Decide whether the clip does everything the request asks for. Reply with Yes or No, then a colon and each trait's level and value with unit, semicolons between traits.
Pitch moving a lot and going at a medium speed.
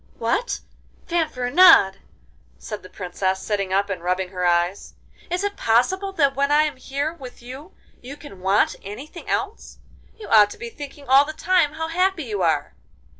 Yes: wide, 8.4 semitones; average, 175 wpm